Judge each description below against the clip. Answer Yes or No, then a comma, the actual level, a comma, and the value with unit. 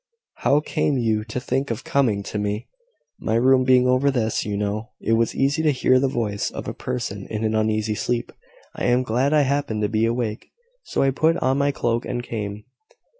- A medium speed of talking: No, fast, 210 wpm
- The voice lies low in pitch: Yes, low, 120 Hz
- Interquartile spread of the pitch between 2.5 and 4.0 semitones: Yes, average, 3.6 semitones